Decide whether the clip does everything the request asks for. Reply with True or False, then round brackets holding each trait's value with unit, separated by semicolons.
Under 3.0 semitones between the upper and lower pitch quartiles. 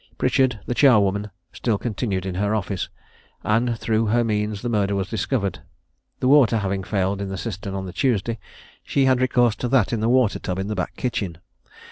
False (3.6 semitones)